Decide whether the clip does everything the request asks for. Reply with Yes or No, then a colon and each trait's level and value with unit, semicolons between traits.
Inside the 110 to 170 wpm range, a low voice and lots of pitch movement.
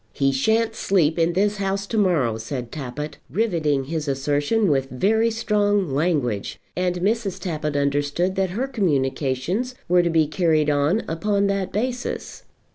No: average, 150 wpm; medium, 170 Hz; wide, 6.0 semitones